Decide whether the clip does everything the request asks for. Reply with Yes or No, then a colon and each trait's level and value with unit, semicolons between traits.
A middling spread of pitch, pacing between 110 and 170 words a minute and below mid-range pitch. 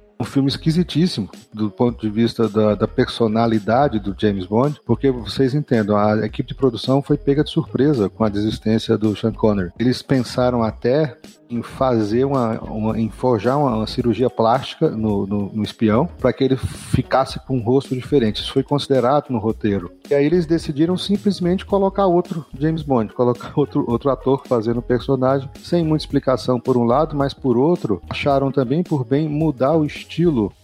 No: average, 4.5 semitones; average, 180 wpm; low, 125 Hz